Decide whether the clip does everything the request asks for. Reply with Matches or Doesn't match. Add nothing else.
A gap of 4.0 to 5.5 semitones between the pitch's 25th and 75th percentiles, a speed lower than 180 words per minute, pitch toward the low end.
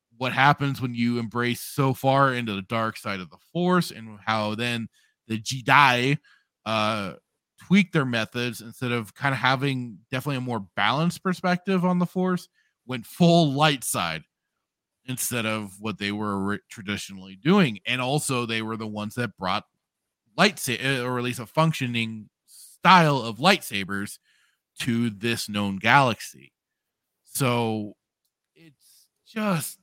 Matches